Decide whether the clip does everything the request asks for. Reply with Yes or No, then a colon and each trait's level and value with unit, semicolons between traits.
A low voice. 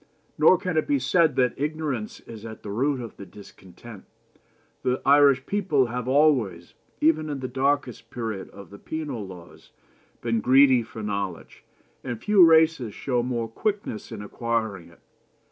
Yes: low, 125 Hz